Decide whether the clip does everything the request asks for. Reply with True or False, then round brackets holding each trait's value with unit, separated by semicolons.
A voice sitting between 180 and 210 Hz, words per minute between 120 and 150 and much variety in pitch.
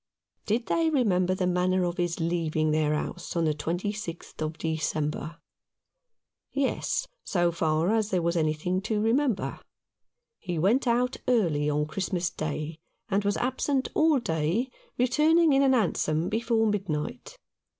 True (185 Hz; 140 wpm; 6.5 semitones)